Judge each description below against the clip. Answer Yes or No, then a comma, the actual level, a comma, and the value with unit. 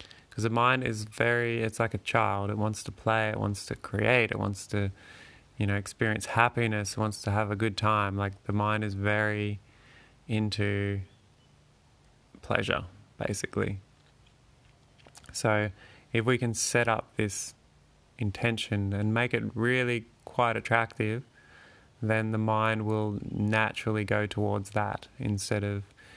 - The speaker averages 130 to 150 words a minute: Yes, average, 145 wpm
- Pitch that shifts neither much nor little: No, narrow, 2.3 semitones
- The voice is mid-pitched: No, low, 110 Hz